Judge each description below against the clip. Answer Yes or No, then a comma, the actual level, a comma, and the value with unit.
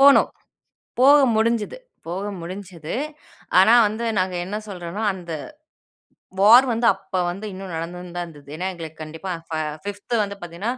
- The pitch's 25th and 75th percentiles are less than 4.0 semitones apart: Yes, average, 3.4 semitones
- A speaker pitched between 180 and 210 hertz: Yes, high, 190 Hz